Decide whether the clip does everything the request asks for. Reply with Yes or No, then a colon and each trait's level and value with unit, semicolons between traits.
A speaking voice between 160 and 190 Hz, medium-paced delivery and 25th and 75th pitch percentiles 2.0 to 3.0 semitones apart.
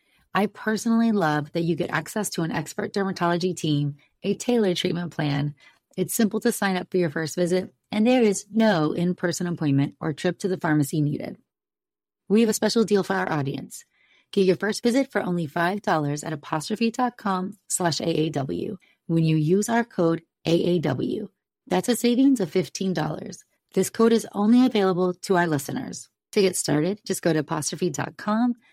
No: medium, 185 Hz; average, 170 wpm; average, 4.5 semitones